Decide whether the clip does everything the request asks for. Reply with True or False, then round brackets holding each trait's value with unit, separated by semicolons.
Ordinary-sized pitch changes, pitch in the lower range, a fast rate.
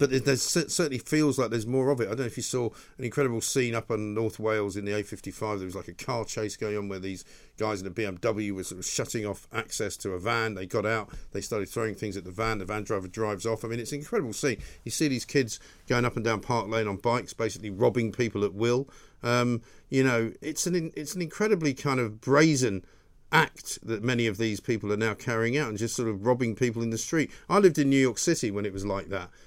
True (3.7 semitones; 115 Hz; 260 wpm)